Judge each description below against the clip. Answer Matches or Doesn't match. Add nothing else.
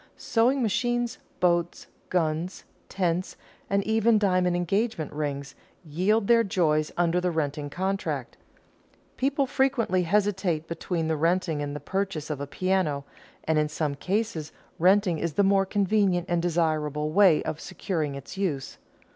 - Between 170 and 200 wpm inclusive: Doesn't match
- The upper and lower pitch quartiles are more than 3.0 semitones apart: Matches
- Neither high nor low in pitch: Matches